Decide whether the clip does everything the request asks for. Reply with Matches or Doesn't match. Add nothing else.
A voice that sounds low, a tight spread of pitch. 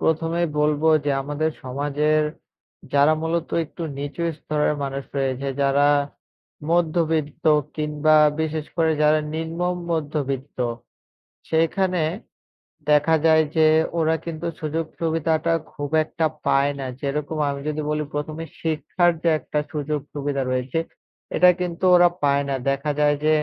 Doesn't match